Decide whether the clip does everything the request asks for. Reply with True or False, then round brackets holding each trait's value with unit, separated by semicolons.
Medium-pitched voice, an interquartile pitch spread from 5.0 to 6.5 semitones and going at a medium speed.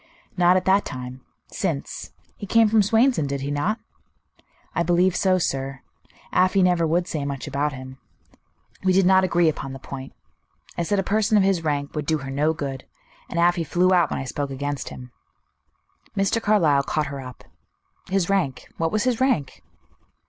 True (165 Hz; 5.4 semitones; 185 wpm)